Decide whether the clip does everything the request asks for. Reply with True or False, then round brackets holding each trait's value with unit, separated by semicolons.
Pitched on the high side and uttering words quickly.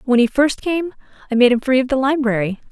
True (260 Hz; 245 wpm)